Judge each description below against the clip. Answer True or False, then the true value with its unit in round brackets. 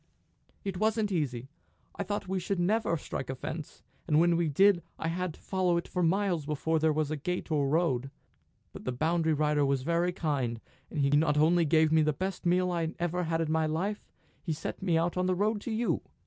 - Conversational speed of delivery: False (220 wpm)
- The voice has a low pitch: False (165 Hz)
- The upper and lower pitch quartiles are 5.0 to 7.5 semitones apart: False (3.1 semitones)